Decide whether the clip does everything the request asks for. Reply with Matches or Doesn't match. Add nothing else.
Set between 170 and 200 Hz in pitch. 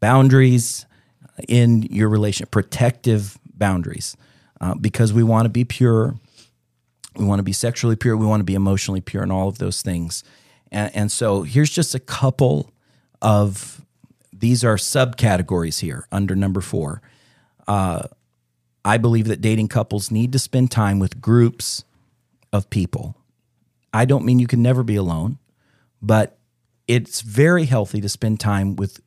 Doesn't match